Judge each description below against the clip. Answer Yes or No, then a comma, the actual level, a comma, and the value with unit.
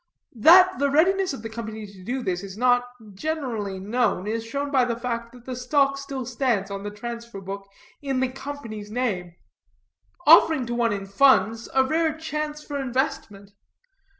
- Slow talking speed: No, average, 175 wpm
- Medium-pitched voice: No, high, 245 Hz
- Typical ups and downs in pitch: Yes, average, 4.8 semitones